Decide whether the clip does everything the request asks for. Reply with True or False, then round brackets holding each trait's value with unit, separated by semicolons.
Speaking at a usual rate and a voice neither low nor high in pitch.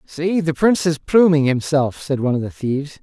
False (220 wpm; 155 Hz)